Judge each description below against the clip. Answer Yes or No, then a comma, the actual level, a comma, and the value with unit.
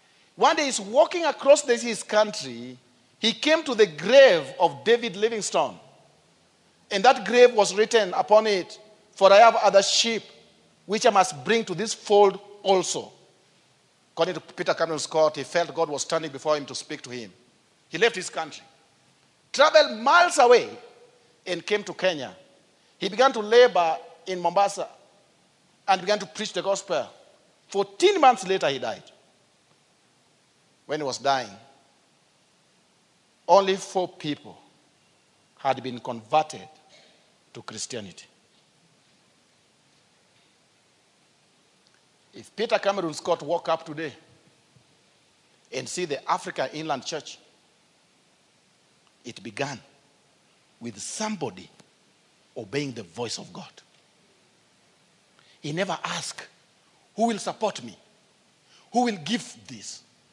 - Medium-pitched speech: No, high, 195 Hz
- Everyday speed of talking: No, slow, 125 wpm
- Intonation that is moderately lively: No, wide, 6.0 semitones